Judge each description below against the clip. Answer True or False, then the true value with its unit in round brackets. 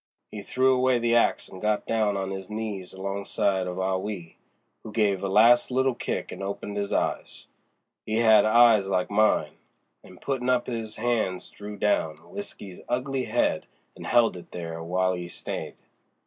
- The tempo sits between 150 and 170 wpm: True (165 wpm)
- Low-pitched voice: True (105 Hz)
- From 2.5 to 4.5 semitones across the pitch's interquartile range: True (3.8 semitones)